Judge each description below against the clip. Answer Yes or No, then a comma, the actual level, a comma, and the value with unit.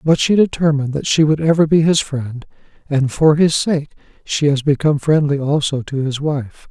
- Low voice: No, medium, 145 Hz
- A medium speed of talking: Yes, average, 195 wpm